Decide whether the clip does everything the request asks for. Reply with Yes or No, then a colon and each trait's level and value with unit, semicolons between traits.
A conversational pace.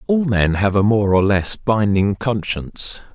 Yes: average, 170 wpm